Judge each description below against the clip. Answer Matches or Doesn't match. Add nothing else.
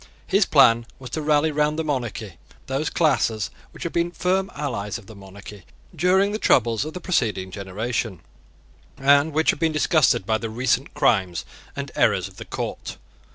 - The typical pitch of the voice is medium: Doesn't match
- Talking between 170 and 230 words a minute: Matches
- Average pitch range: Doesn't match